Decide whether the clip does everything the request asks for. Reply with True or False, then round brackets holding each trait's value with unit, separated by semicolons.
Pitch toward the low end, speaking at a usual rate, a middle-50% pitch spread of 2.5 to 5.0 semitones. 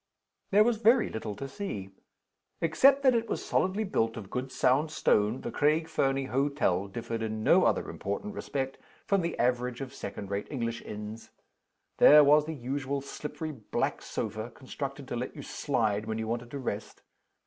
False (130 Hz; 175 wpm; 5.4 semitones)